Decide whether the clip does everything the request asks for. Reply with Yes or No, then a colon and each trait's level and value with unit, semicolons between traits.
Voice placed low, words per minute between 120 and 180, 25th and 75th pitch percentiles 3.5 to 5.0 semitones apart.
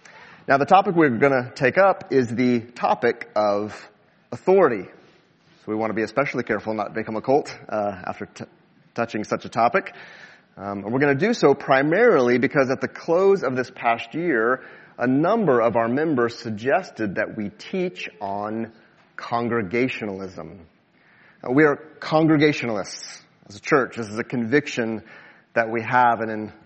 Yes: low, 120 Hz; average, 165 wpm; average, 4.3 semitones